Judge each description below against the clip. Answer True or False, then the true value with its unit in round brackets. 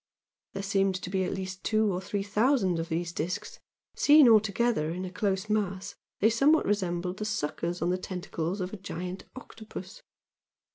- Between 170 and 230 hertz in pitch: True (190 Hz)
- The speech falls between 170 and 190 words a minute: True (180 wpm)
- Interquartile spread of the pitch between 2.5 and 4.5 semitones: True (2.9 semitones)